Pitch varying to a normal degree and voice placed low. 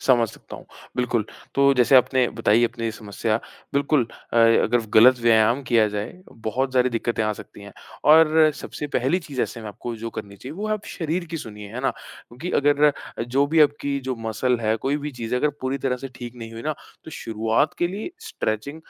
Yes: average, 4.1 semitones; low, 125 Hz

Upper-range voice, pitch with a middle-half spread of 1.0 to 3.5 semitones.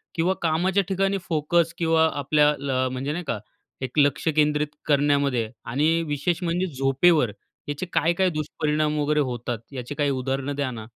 No: medium, 150 Hz; average, 3.1 semitones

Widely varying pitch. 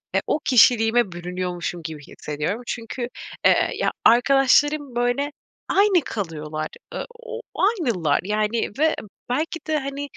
Yes: wide, 8.2 semitones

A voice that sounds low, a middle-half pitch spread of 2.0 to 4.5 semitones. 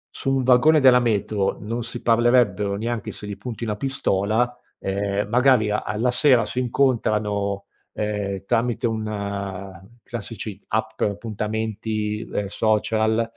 Yes: low, 110 Hz; average, 2.8 semitones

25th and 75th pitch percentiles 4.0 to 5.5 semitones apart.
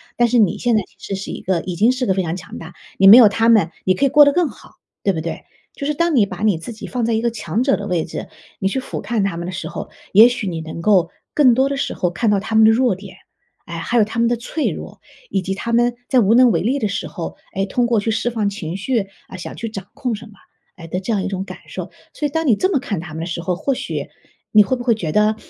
Yes: average, 4.4 semitones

